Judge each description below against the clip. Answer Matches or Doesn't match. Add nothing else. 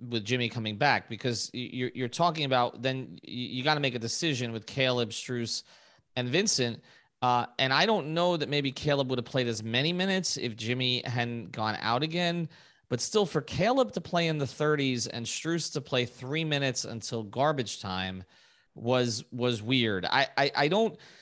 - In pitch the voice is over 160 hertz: Doesn't match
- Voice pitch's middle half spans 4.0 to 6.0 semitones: Matches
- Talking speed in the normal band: Matches